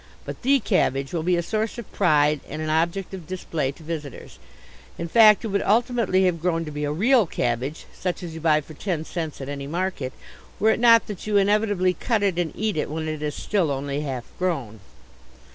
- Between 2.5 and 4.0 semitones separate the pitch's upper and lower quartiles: No, average, 5.1 semitones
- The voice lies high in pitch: No, medium, 170 Hz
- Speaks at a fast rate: Yes, fast, 215 wpm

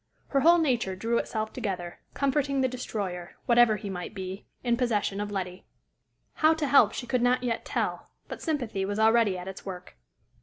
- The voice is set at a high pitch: Yes, high, 225 Hz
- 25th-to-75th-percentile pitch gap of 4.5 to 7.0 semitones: Yes, average, 4.8 semitones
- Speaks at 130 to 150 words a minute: No, average, 185 wpm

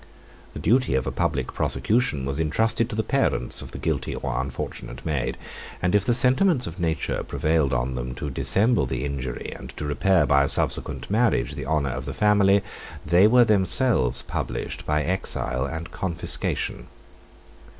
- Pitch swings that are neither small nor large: No, wide, 7.7 semitones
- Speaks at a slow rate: No, average, 170 wpm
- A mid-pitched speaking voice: No, very low, 80 Hz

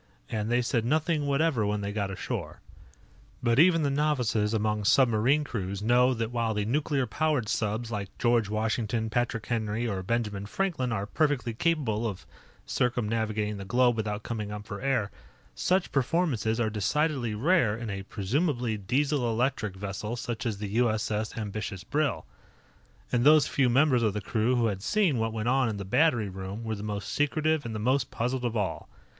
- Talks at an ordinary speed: Yes, average, 180 wpm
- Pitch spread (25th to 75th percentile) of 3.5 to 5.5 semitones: Yes, average, 3.9 semitones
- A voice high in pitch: No, low, 115 Hz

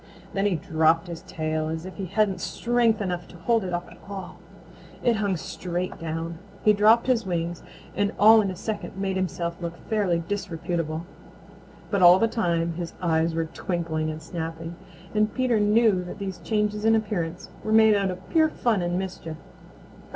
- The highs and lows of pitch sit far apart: No, average, 3.9 semitones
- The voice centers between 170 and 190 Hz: Yes, medium, 185 Hz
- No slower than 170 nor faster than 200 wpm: Yes, average, 180 wpm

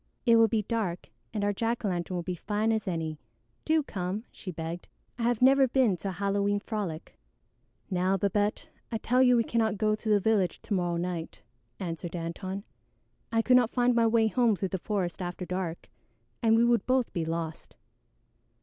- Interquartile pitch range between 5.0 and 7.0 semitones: No, average, 4.2 semitones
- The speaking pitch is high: Yes, high, 205 Hz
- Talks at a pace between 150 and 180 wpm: No, average, 195 wpm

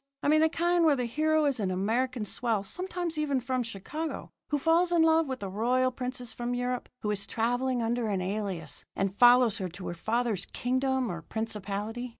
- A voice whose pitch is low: No, high, 245 Hz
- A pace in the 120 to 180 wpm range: No, average, 195 wpm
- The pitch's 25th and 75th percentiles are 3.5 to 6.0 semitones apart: Yes, average, 4.9 semitones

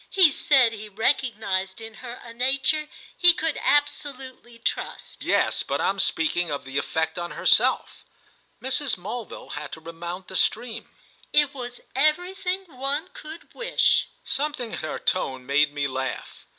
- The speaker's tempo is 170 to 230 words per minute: No, average, 150 wpm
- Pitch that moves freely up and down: Yes, wide, 8.6 semitones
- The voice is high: Yes, high, 240 Hz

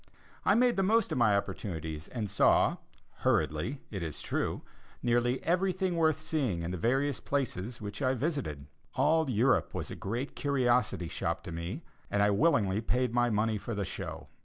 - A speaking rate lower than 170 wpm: No, average, 175 wpm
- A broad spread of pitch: Yes, wide, 6.2 semitones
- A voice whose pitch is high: No, low, 120 Hz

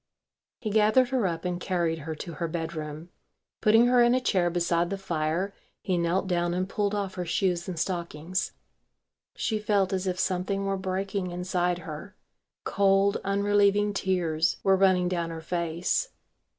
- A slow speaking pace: No, average, 165 wpm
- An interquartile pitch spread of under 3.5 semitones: Yes, narrow, 2.6 semitones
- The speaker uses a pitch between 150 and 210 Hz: Yes, medium, 185 Hz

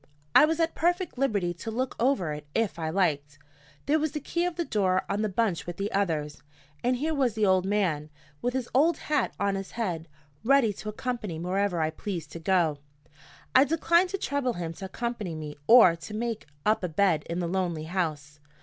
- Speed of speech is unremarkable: No, fast, 210 wpm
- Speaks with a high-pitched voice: Yes, high, 200 Hz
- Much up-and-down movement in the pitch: Yes, wide, 7.0 semitones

